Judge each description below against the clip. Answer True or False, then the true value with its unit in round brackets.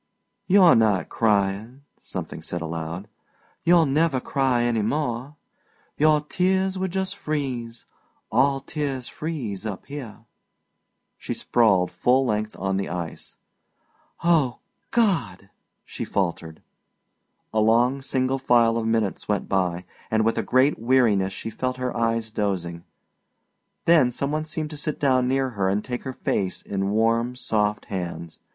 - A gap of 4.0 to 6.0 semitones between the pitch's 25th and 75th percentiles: True (5.4 semitones)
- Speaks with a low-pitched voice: True (120 Hz)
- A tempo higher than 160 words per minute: False (140 wpm)